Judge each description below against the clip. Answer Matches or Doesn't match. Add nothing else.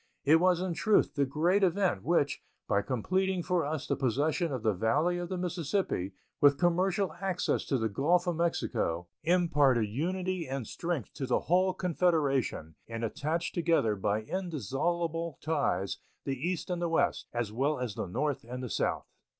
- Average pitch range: Doesn't match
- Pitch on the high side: Doesn't match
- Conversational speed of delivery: Matches